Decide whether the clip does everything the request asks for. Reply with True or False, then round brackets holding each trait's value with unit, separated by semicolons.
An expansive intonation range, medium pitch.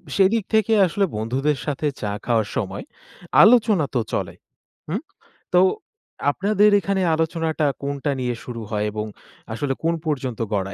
True (8.4 semitones; 150 Hz)